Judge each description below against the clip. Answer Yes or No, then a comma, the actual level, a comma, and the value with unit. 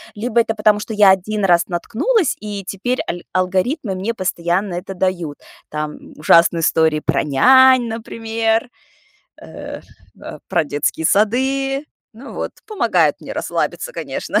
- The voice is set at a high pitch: Yes, high, 210 Hz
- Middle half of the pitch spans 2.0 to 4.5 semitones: No, average, 5.3 semitones